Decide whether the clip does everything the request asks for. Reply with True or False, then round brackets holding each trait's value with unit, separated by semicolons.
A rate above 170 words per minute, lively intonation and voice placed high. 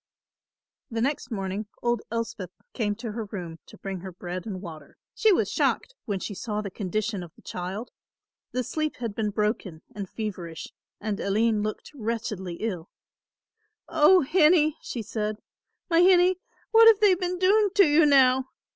False (165 wpm; 7.3 semitones; 220 Hz)